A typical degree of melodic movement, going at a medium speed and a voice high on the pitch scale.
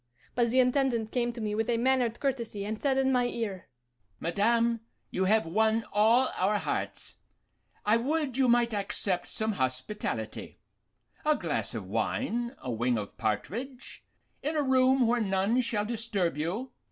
Yes: average, 3.7 semitones; average, 160 wpm; high, 230 Hz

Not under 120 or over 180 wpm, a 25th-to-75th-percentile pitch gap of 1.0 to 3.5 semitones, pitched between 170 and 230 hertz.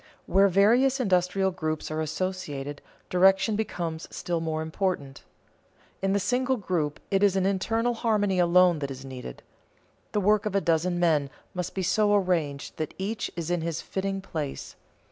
No: average, 165 wpm; average, 3.9 semitones; medium, 185 Hz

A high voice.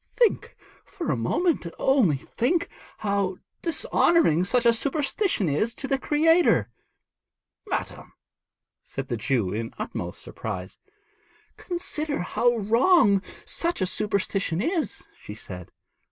Yes: high, 235 Hz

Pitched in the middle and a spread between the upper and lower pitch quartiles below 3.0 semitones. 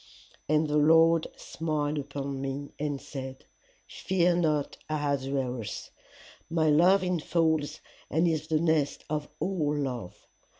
Yes: medium, 150 Hz; narrow, 2.4 semitones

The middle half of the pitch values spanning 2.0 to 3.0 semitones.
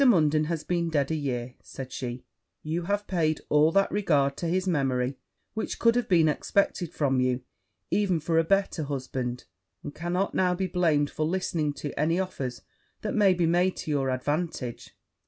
No: average, 4.6 semitones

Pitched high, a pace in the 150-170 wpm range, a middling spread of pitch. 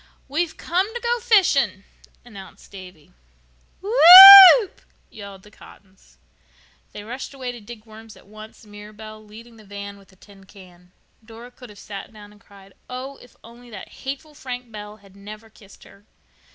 Yes: high, 215 Hz; average, 165 wpm; average, 4.4 semitones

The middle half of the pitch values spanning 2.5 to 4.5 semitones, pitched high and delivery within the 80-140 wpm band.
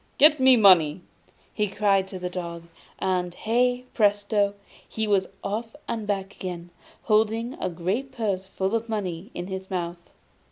No: average, 3.4 semitones; high, 200 Hz; average, 155 wpm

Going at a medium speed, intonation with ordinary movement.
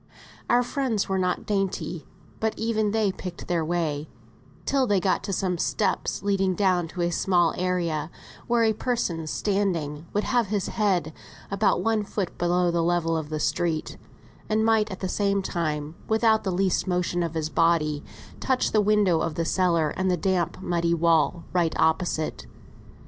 Yes: average, 170 wpm; average, 3.6 semitones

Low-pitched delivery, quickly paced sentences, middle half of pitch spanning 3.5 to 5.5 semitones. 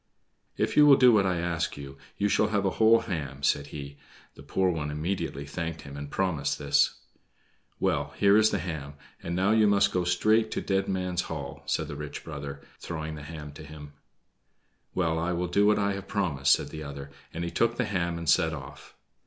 Yes: very low, 85 Hz; fast, 210 wpm; average, 5.2 semitones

